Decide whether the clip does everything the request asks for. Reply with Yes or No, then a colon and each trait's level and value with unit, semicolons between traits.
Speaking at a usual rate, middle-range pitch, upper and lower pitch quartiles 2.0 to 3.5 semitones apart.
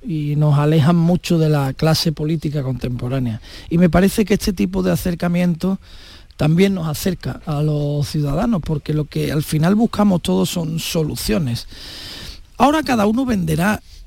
No: average, 155 wpm; medium, 160 Hz; average, 4.1 semitones